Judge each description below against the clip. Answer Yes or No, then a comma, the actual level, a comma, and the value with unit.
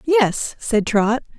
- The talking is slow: Yes, slow, 130 wpm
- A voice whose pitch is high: Yes, high, 225 Hz